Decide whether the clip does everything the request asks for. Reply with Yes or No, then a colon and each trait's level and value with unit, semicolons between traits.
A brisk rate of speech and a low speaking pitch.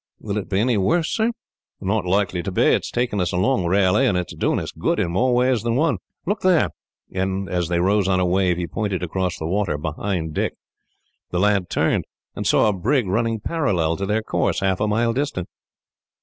Yes: fast, 220 wpm; low, 100 Hz